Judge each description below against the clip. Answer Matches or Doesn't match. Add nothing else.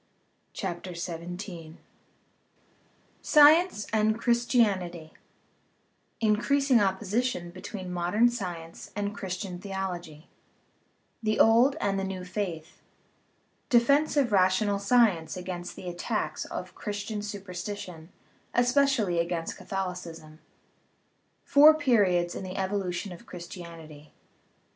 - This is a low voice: Doesn't match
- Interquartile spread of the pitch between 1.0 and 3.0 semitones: Doesn't match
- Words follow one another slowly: Matches